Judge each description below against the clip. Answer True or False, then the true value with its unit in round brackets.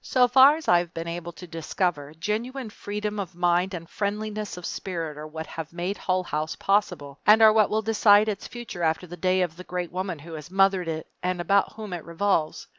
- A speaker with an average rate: False (220 wpm)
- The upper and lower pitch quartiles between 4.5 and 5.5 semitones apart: False (3.8 semitones)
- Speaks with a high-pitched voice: False (180 Hz)